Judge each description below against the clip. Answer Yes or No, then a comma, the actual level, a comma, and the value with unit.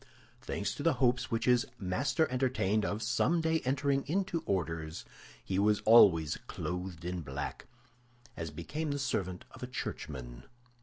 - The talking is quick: No, average, 145 wpm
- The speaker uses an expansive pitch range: Yes, wide, 7.7 semitones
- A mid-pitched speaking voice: No, low, 110 Hz